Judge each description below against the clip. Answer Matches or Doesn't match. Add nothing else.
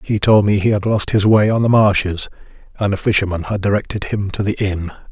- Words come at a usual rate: Doesn't match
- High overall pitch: Doesn't match